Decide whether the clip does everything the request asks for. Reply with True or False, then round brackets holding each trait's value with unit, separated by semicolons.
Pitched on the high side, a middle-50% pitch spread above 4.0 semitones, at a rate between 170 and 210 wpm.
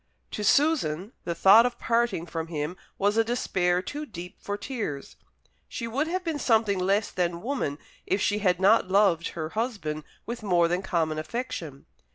True (195 Hz; 5.3 semitones; 175 wpm)